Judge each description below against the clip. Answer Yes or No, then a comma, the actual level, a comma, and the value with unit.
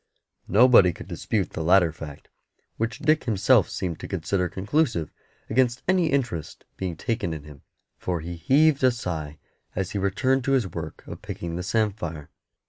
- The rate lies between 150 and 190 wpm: Yes, average, 165 wpm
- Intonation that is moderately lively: No, wide, 7.0 semitones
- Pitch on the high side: No, very low, 95 Hz